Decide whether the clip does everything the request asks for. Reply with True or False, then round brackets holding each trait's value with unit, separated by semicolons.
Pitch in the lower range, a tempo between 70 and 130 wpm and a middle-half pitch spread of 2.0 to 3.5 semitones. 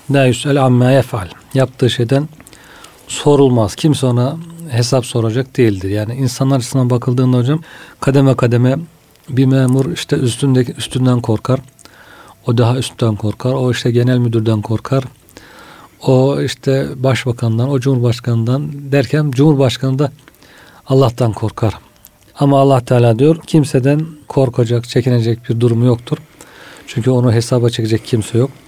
True (130 Hz; 120 wpm; 2.4 semitones)